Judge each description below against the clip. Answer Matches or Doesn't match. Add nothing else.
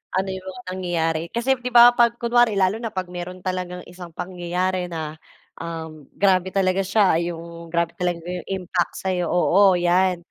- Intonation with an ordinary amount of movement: Doesn't match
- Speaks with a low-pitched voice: Doesn't match